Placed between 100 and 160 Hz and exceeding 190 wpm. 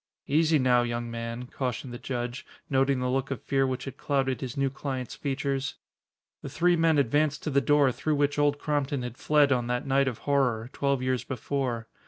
Yes: low, 135 Hz; average, 200 wpm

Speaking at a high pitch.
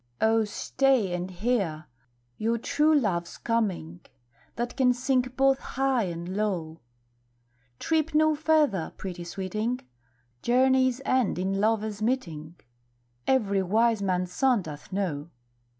Yes: high, 215 Hz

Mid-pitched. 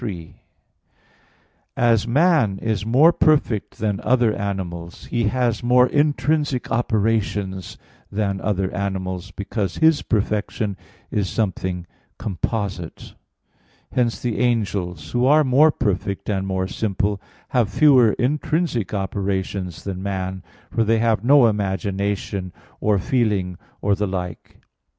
No: low, 105 Hz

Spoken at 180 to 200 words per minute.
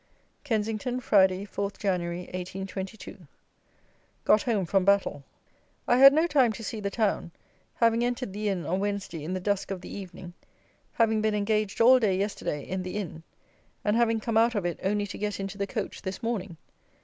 Yes: average, 185 wpm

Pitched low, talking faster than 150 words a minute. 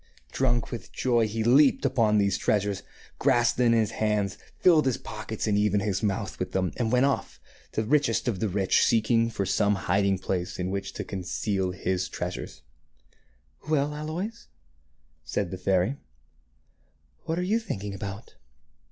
Yes: low, 105 Hz; average, 170 wpm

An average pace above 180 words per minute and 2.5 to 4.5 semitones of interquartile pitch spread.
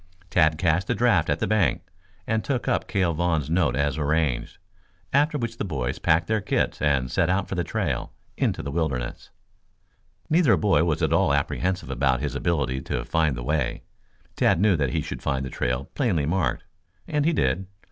No: average, 190 wpm; wide, 5.6 semitones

